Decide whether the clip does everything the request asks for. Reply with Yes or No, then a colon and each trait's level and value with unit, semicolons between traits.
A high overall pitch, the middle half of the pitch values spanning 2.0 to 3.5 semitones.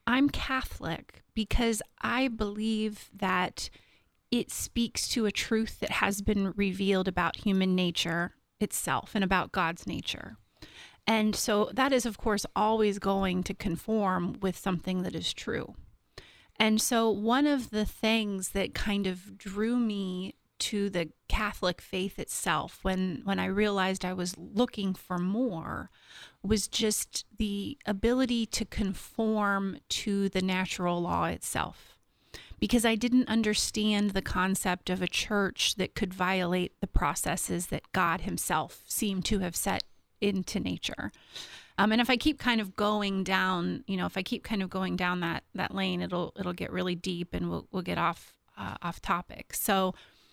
Yes: high, 200 Hz; average, 2.8 semitones